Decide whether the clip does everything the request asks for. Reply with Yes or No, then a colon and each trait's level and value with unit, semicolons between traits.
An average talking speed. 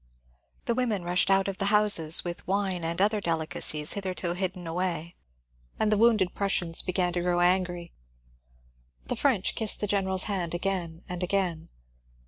Yes: average, 155 wpm